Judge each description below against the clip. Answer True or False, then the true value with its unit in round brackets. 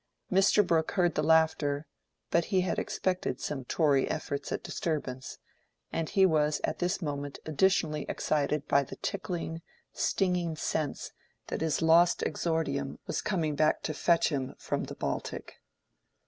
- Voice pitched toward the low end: False (160 Hz)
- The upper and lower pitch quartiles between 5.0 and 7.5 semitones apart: False (3.2 semitones)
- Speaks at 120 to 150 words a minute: True (145 wpm)